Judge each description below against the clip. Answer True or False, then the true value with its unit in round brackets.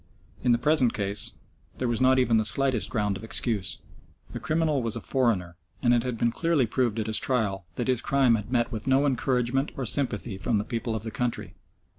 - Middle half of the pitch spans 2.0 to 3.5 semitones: True (3.0 semitones)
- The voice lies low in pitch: True (120 Hz)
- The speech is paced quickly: True (215 wpm)